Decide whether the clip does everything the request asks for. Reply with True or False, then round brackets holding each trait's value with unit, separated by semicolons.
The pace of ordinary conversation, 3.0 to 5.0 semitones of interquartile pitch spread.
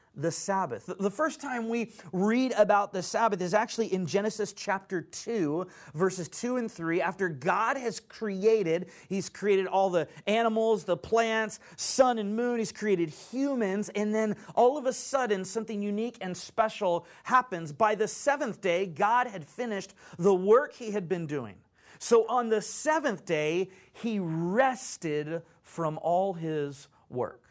True (155 wpm; 4.4 semitones)